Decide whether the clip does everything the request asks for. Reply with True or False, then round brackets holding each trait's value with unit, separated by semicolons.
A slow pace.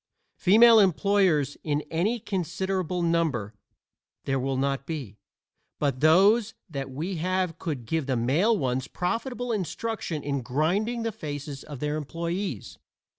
True (130 wpm)